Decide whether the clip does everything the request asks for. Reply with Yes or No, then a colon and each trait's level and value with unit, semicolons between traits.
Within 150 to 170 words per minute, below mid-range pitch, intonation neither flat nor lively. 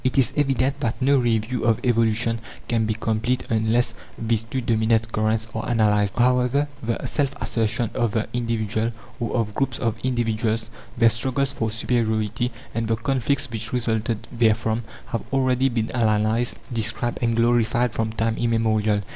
No: average, 155 wpm; low, 115 Hz; narrow, 1.7 semitones